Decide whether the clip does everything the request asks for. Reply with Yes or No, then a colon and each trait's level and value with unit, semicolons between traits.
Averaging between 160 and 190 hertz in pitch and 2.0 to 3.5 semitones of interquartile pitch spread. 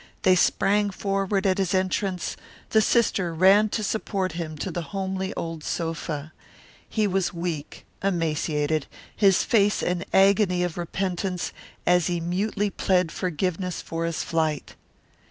Yes: medium, 185 Hz; average, 2.8 semitones